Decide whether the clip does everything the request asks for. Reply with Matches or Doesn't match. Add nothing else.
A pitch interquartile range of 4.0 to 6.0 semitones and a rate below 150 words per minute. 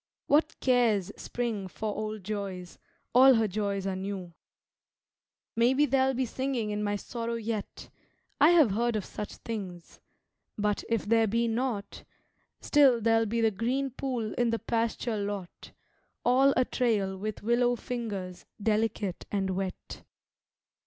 Doesn't match